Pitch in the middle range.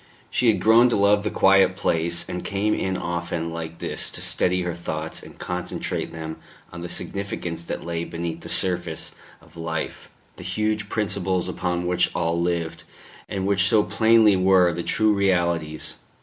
No: very low, 90 Hz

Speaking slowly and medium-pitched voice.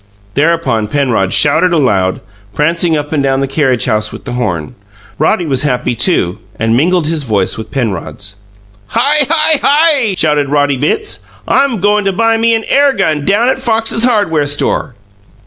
No: average, 165 wpm; medium, 150 Hz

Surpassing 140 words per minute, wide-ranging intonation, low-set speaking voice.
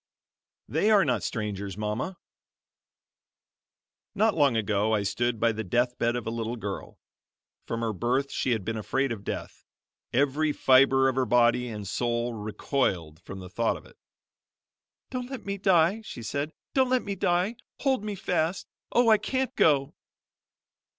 Yes: average, 165 wpm; wide, 8.1 semitones; low, 125 Hz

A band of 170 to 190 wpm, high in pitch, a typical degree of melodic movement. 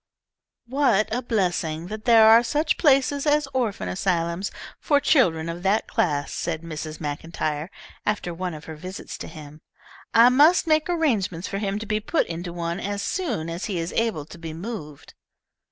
No: average, 175 wpm; high, 195 Hz; wide, 6.4 semitones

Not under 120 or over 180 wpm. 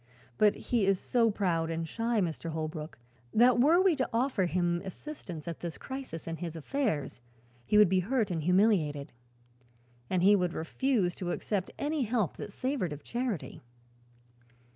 Yes: average, 165 wpm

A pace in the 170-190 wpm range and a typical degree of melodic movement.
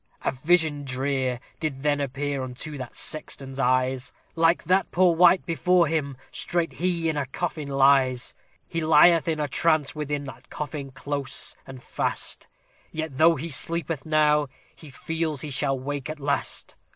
No: average, 160 wpm; average, 3.2 semitones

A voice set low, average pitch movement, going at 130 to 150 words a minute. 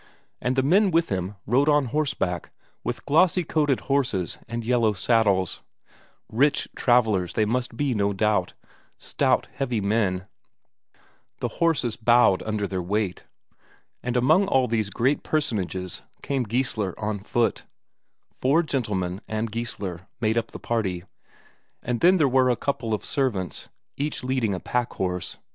Yes: low, 115 Hz; average, 5.0 semitones; average, 145 wpm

